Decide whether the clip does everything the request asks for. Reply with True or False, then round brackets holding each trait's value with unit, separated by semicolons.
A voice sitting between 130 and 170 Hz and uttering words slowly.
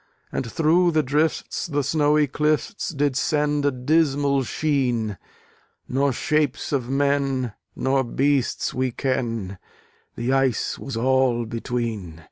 True (135 Hz; 120 wpm)